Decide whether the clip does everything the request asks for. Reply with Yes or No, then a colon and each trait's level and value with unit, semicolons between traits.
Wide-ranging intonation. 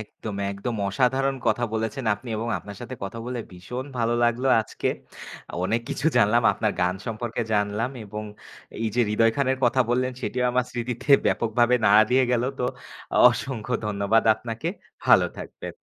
No: average, 2.7 semitones